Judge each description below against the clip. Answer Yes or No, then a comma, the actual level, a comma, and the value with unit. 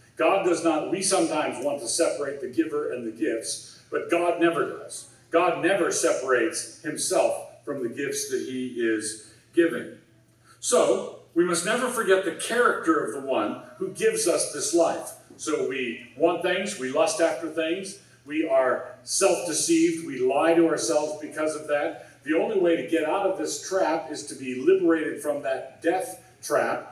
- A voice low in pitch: No, medium, 170 Hz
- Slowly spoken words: No, average, 175 wpm